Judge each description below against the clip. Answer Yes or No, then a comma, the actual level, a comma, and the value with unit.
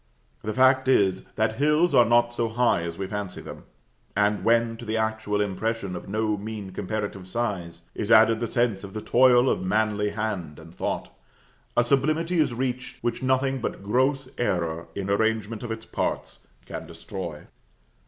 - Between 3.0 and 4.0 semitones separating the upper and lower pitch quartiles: Yes, average, 3.4 semitones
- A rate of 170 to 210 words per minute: Yes, average, 175 wpm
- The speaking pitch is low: Yes, low, 110 Hz